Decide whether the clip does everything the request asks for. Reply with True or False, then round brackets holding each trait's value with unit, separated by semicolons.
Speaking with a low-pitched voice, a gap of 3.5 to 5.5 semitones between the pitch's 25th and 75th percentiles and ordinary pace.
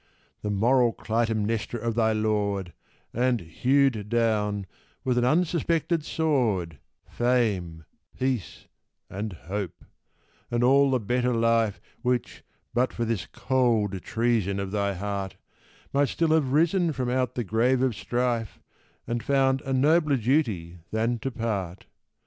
False (115 Hz; 4.0 semitones; 130 wpm)